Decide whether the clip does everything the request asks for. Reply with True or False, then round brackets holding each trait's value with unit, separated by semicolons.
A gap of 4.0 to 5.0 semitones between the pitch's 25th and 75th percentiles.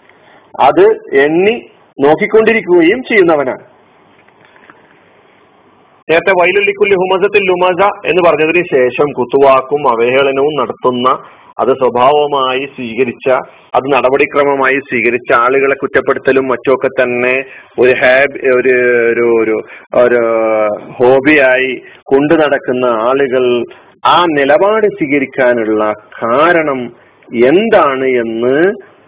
True (4.7 semitones)